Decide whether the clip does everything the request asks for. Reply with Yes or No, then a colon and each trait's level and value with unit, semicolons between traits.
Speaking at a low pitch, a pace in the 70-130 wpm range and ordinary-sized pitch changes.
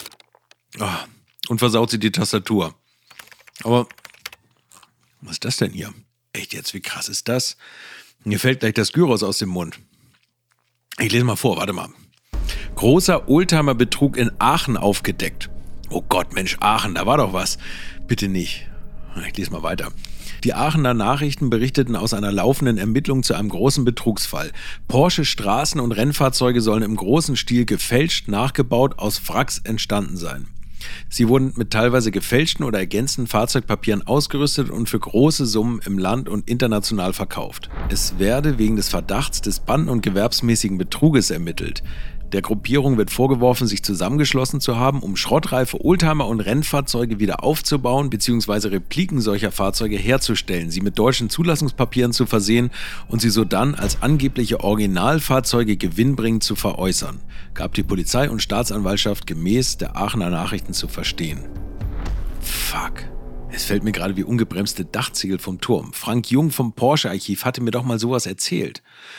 No: low, 115 Hz; average, 150 wpm; average, 4.2 semitones